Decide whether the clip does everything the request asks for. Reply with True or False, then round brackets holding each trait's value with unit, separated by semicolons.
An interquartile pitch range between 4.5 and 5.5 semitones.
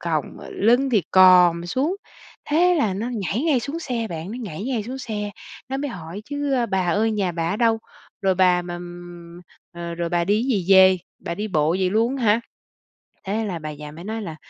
True (5.1 semitones)